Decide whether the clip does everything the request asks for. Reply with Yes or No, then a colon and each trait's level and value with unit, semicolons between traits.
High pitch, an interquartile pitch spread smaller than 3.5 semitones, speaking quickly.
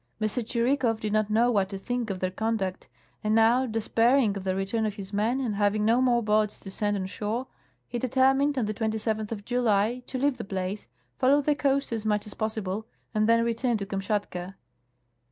Yes: high, 220 Hz; average, 2.8 semitones; fast, 210 wpm